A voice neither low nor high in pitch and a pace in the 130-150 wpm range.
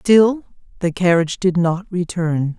Yes: medium, 180 Hz; average, 140 wpm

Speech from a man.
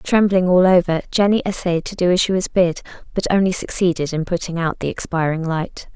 No: female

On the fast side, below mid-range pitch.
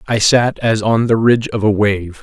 Yes: fast, 245 wpm; low, 110 Hz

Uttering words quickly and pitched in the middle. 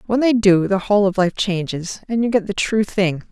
No: fast, 255 wpm; high, 200 Hz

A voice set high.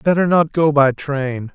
No: medium, 150 Hz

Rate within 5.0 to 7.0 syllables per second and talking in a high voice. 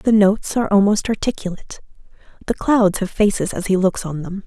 Yes: 5.9 syllables/s; high, 200 Hz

